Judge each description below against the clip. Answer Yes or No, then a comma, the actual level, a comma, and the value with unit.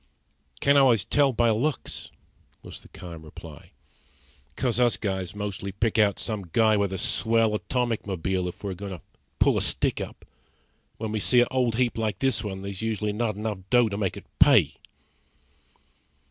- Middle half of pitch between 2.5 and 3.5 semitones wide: Yes, average, 3.2 semitones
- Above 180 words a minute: No, average, 175 wpm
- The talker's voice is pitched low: Yes, low, 105 Hz